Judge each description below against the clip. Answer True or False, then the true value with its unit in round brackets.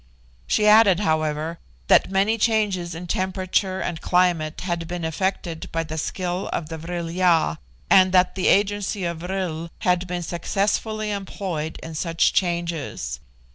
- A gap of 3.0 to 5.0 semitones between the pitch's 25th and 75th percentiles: False (2.6 semitones)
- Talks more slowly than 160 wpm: True (145 wpm)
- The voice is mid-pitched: True (180 Hz)